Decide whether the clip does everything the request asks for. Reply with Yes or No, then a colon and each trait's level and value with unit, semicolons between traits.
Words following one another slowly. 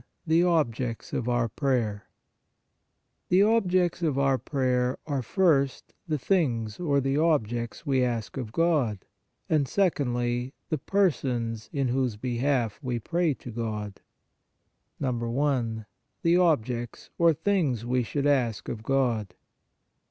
Yes: slow, 130 wpm